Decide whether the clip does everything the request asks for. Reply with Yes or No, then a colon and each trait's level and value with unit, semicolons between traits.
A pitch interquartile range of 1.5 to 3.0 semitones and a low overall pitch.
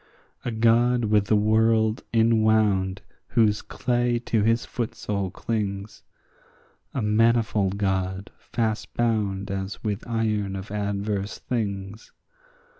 Yes: narrow, 2.4 semitones; low, 105 Hz